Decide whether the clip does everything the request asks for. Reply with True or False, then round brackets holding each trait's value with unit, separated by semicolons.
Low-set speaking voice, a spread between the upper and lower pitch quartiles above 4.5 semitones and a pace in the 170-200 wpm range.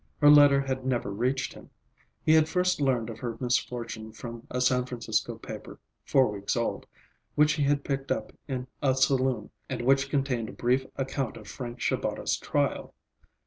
False (130 Hz; 2.7 semitones; 175 wpm)